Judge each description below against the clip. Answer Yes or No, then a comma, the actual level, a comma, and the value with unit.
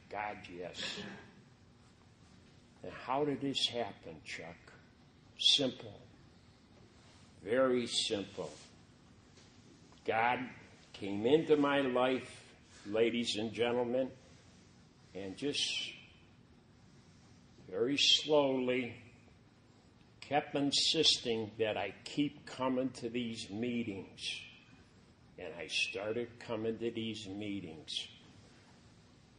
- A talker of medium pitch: No, low, 120 Hz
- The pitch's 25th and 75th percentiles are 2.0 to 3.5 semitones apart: Yes, narrow, 2.6 semitones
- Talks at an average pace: No, slow, 80 wpm